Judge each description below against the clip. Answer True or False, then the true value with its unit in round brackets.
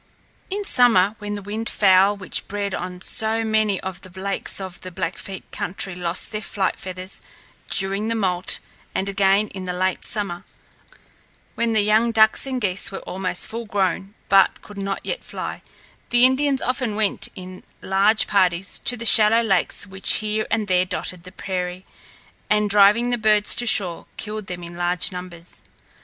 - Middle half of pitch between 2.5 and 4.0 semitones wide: True (2.9 semitones)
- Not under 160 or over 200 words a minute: True (170 wpm)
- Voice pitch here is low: False (200 Hz)